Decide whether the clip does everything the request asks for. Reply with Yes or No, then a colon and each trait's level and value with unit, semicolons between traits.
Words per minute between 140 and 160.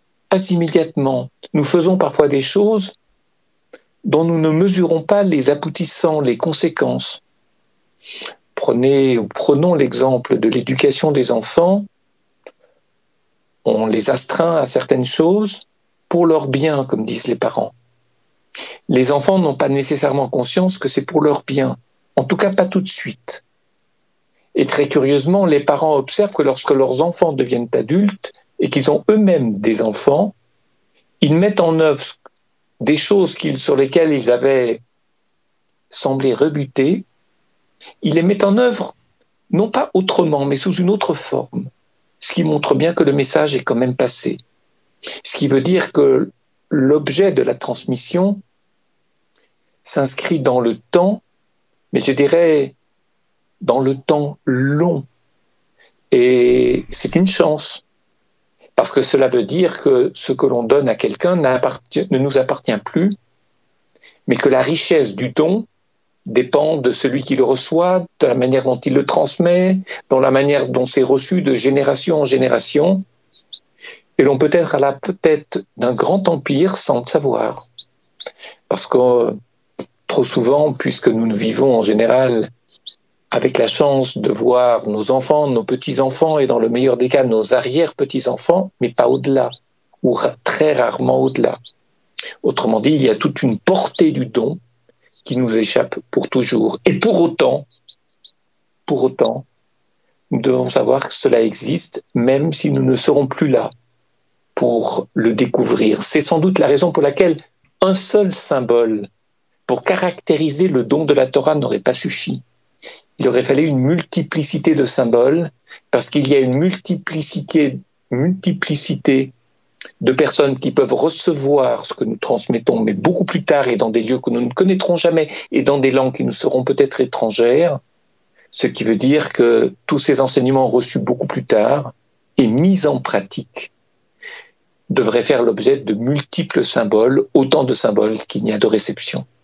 Yes: average, 155 wpm